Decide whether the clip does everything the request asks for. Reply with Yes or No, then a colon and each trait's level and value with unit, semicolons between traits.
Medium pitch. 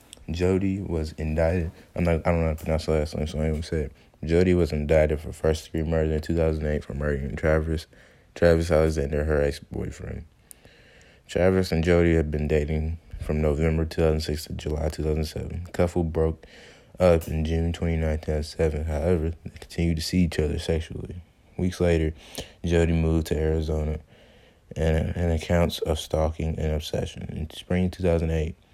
No: very low, 80 Hz